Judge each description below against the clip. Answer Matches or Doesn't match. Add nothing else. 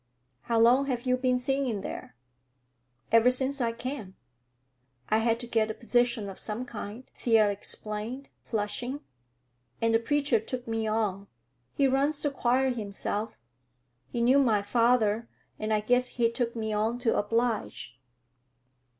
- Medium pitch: Doesn't match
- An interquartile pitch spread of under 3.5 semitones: Matches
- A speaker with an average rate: Matches